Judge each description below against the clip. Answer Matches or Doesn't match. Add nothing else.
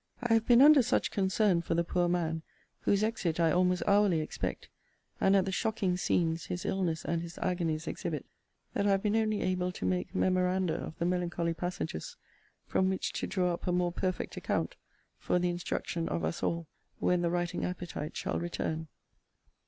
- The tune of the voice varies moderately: Doesn't match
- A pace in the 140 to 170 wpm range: Doesn't match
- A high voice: Doesn't match